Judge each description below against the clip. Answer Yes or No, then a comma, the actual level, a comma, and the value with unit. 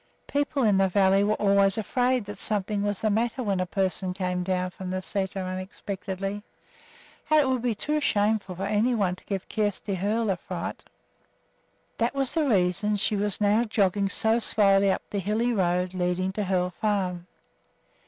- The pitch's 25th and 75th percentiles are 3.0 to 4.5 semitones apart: No, narrow, 2.6 semitones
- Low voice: No, high, 200 Hz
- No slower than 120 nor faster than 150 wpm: No, average, 180 wpm